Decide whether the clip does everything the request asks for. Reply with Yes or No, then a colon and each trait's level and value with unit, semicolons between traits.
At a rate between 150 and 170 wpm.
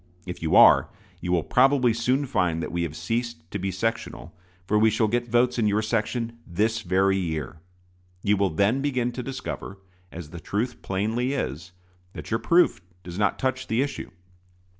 No: average, 185 wpm